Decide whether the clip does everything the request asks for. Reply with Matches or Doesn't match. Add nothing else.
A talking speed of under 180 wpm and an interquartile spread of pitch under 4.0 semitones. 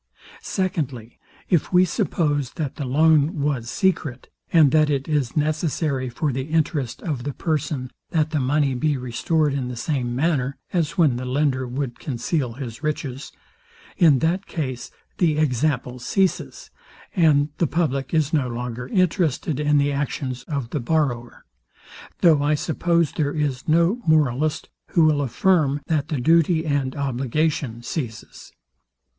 Matches